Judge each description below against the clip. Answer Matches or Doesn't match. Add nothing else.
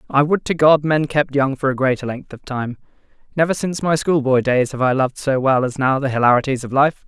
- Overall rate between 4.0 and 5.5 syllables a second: Doesn't match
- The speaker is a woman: Doesn't match